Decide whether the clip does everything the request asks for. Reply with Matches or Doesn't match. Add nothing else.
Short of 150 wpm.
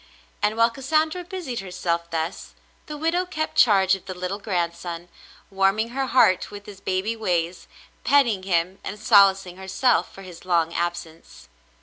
Doesn't match